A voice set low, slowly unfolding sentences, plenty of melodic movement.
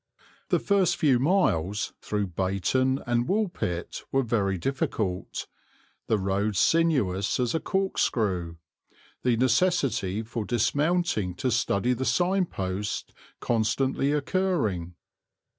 Yes: low, 120 Hz; slow, 110 wpm; wide, 7.1 semitones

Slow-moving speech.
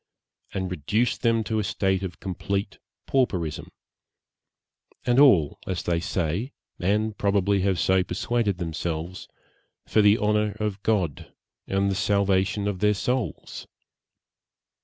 Yes: slow, 130 wpm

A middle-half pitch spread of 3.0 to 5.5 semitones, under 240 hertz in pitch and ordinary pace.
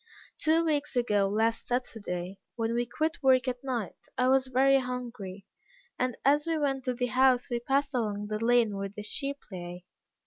No: average, 4.1 semitones; high, 245 Hz; average, 180 wpm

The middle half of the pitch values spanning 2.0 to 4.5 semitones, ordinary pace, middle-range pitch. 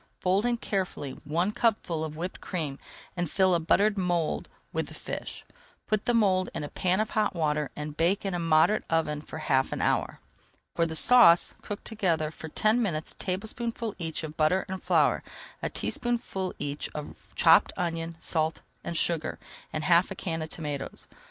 Yes: average, 4.0 semitones; average, 185 wpm; medium, 170 Hz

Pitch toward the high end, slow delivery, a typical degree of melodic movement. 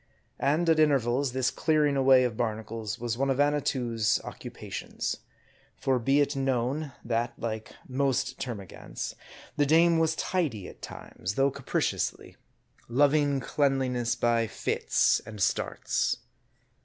No: low, 130 Hz; slow, 125 wpm; average, 3.6 semitones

